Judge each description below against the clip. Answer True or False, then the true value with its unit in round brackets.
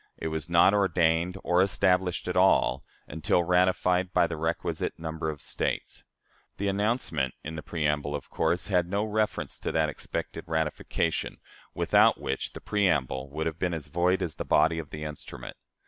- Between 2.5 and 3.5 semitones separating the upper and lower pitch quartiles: True (2.8 semitones)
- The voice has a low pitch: True (85 Hz)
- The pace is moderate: True (165 wpm)